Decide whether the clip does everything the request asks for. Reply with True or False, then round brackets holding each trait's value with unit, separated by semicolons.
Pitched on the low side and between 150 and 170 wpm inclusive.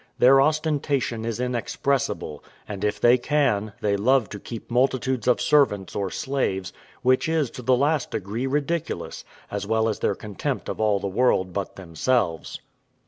True (120 Hz; 160 wpm)